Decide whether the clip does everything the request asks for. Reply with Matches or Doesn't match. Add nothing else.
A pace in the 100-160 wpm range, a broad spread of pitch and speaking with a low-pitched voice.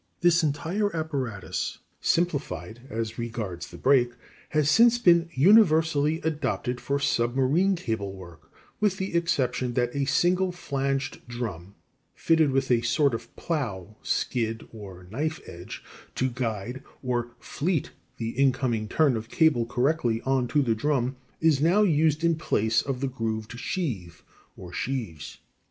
Matches